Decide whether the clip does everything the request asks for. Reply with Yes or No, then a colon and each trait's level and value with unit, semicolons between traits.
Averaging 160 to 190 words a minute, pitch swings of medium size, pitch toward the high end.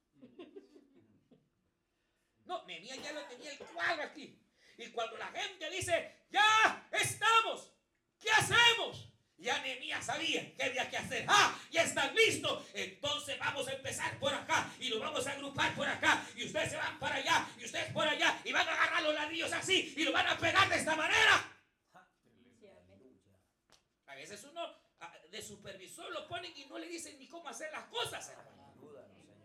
Yes: average, 165 wpm; average, 4.4 semitones; very high, 310 Hz